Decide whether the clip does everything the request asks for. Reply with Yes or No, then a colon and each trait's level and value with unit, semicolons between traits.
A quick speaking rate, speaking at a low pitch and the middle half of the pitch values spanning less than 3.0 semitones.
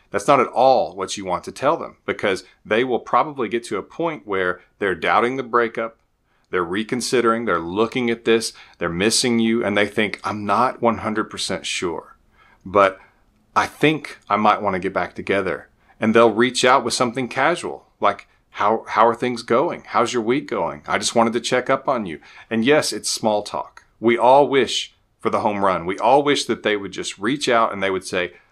Yes: fast, 210 wpm; low, 115 Hz; narrow, 2.4 semitones